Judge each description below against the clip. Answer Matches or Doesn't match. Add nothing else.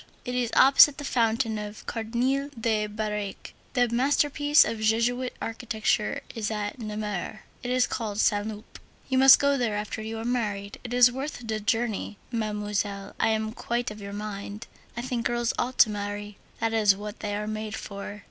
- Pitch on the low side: Doesn't match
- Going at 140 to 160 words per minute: Doesn't match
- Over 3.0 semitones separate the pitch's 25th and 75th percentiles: Doesn't match